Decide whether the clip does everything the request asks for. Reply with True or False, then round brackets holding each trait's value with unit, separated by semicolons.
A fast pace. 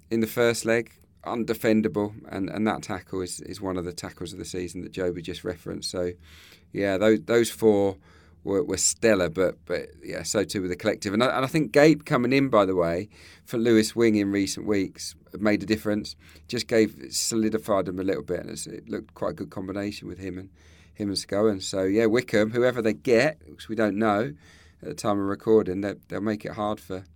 True (215 wpm)